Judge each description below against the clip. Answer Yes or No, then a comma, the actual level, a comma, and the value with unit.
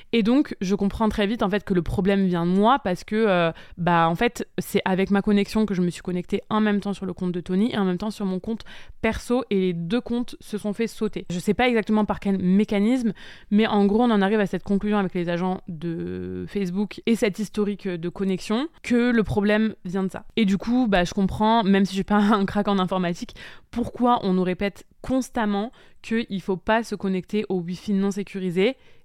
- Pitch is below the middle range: No, high, 200 Hz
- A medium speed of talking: No, fast, 240 wpm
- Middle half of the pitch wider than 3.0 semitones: No, average, 2.7 semitones